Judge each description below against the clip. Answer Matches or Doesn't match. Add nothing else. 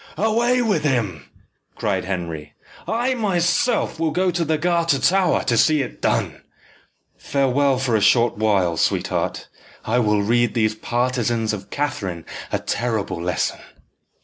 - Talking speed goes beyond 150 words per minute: Doesn't match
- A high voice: Doesn't match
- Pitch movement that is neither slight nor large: Doesn't match